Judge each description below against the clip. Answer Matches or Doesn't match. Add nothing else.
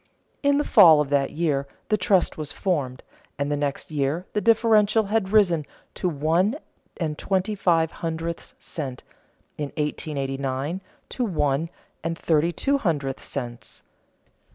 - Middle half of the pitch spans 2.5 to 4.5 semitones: Doesn't match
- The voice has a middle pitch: Matches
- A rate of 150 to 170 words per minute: Doesn't match